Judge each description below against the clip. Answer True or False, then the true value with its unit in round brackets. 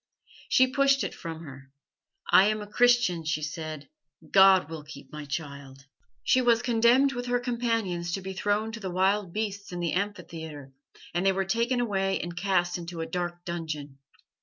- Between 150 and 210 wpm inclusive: True (180 wpm)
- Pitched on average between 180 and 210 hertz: True (185 Hz)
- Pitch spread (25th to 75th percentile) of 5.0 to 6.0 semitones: True (5.4 semitones)